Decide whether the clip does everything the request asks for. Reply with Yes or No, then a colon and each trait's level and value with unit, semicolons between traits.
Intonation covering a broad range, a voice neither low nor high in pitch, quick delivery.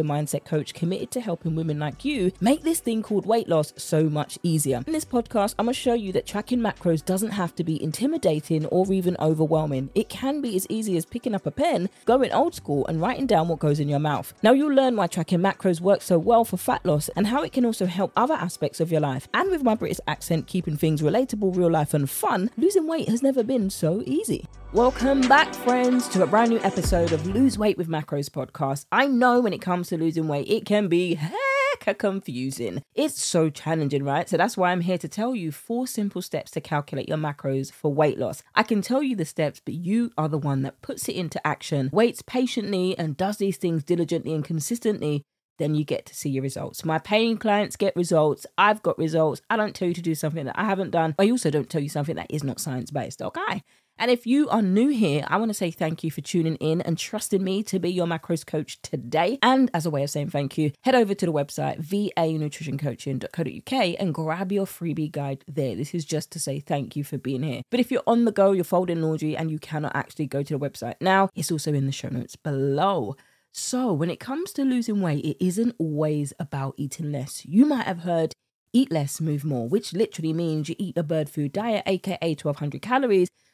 Yes: wide, 5.9 semitones; medium, 170 Hz; fast, 230 wpm